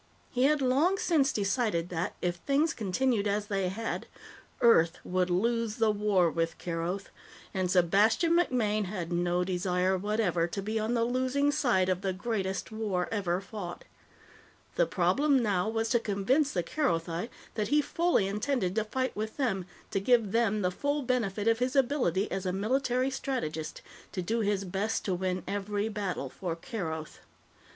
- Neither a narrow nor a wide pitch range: Yes, average, 5.0 semitones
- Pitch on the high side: Yes, high, 210 Hz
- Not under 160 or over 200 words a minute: Yes, average, 165 wpm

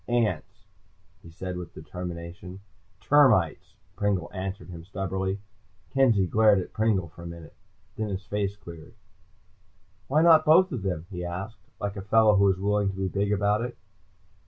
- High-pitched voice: No, low, 100 Hz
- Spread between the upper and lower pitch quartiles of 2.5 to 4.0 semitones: Yes, average, 3.0 semitones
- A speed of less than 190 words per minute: Yes, average, 160 wpm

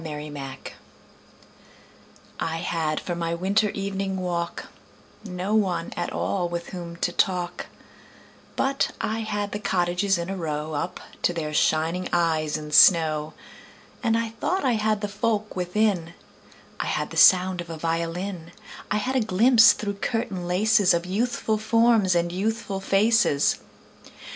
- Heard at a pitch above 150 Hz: Yes, medium, 185 Hz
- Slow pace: No, average, 150 wpm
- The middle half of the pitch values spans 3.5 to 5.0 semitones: Yes, average, 4.0 semitones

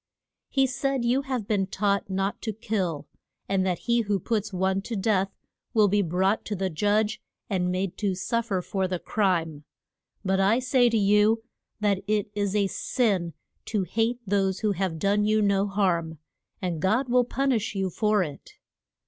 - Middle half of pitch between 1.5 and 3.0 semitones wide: Yes, narrow, 2.6 semitones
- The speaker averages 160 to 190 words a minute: Yes, average, 180 wpm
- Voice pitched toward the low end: No, high, 200 Hz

